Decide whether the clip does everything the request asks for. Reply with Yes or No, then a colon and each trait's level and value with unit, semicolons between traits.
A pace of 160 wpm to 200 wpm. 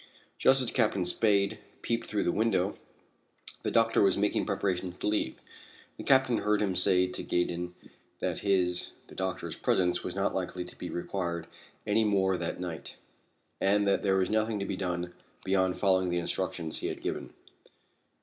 Yes: average, 170 wpm